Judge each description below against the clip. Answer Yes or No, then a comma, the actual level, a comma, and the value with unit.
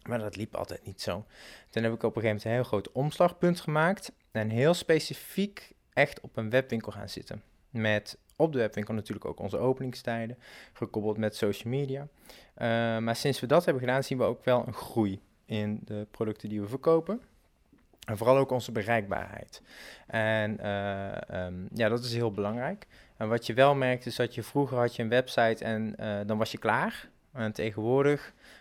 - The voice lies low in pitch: Yes, low, 115 Hz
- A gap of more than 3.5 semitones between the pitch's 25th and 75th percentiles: No, average, 3.2 semitones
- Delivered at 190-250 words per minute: Yes, average, 195 wpm